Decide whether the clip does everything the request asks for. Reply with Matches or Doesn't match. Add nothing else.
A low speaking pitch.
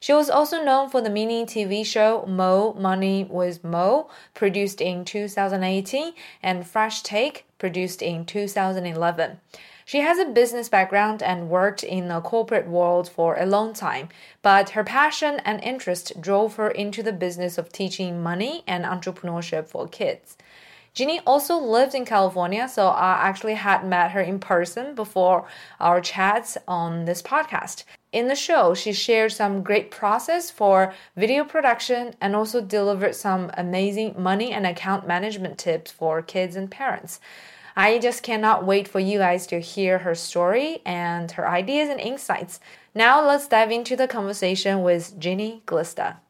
Doesn't match